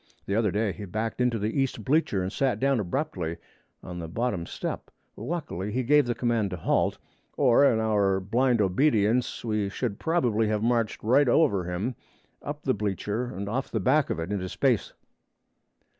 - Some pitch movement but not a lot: Yes, average, 4.2 semitones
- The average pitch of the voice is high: No, low, 110 Hz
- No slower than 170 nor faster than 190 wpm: Yes, average, 180 wpm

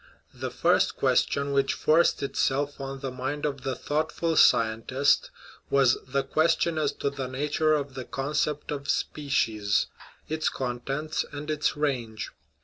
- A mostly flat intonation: Yes, narrow, 2.3 semitones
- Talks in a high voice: No, medium, 140 Hz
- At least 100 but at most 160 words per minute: Yes, average, 145 wpm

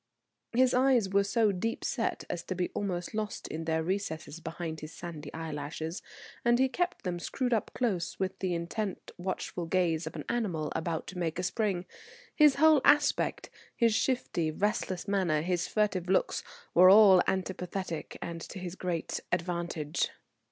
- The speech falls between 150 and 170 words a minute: Yes, average, 165 wpm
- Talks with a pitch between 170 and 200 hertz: Yes, medium, 185 Hz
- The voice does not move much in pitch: No, average, 4.0 semitones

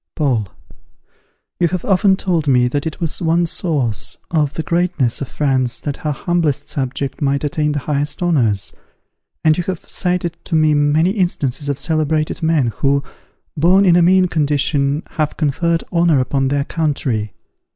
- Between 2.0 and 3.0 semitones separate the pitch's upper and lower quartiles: No, average, 3.4 semitones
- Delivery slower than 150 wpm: No, average, 160 wpm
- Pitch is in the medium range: Yes, medium, 150 Hz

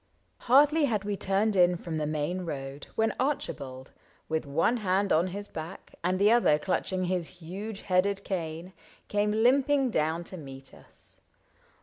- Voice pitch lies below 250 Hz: Yes, medium, 185 Hz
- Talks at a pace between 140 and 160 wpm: Yes, average, 155 wpm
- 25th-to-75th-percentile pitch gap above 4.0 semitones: Yes, average, 4.7 semitones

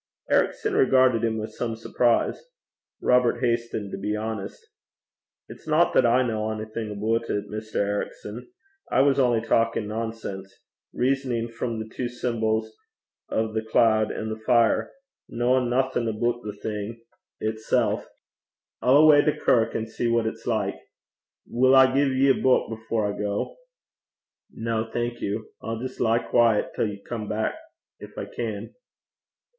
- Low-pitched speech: Yes, low, 115 Hz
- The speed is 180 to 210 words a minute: No, average, 155 wpm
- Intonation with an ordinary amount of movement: No, narrow, 1.9 semitones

